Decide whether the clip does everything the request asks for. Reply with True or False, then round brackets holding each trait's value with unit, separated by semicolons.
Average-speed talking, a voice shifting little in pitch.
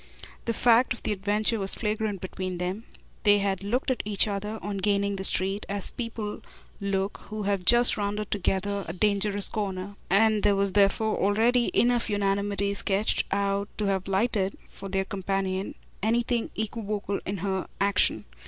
True (160 wpm; 1.6 semitones)